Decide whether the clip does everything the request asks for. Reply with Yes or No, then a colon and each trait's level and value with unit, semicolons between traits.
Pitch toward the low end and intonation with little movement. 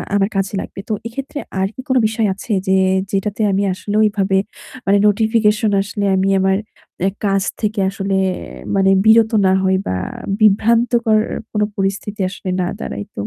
No: high, 205 Hz; narrow, 2.1 semitones